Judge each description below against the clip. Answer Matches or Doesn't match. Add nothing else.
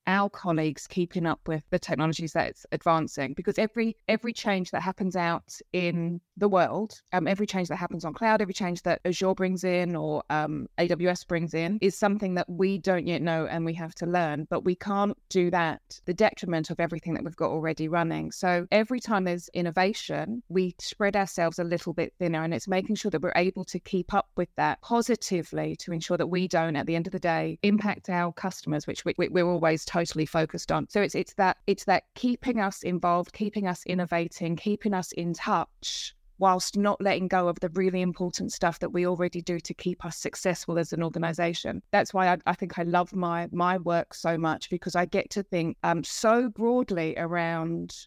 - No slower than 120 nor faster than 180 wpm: Doesn't match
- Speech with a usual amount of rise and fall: Doesn't match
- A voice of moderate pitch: Matches